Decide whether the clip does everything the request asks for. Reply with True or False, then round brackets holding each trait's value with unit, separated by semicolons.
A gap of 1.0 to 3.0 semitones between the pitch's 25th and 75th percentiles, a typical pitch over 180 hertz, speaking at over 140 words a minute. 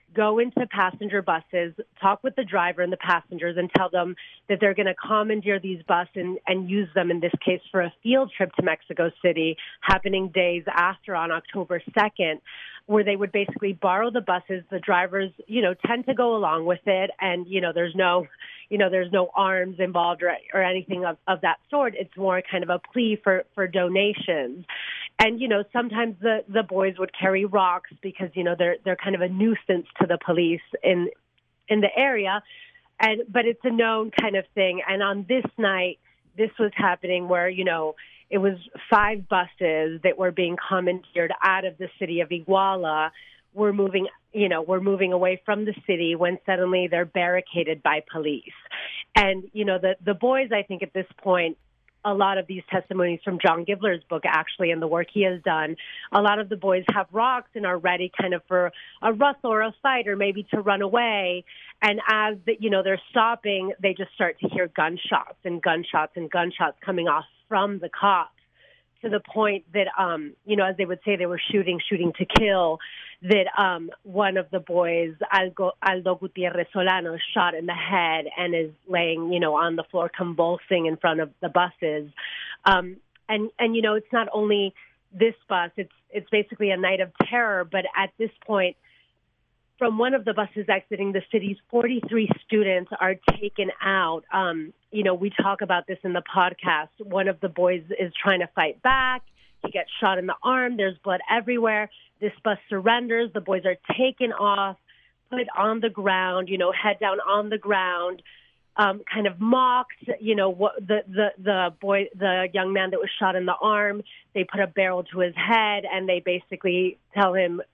True (2.7 semitones; 190 Hz; 200 wpm)